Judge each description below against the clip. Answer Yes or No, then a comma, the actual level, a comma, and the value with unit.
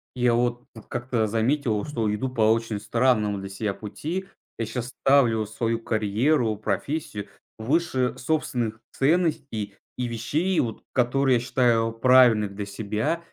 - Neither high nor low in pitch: No, low, 120 Hz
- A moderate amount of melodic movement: Yes, average, 3.3 semitones